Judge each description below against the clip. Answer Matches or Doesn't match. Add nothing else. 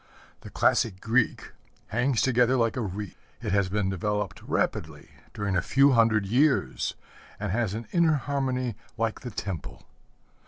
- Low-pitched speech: Matches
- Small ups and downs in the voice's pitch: Doesn't match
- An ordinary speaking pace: Matches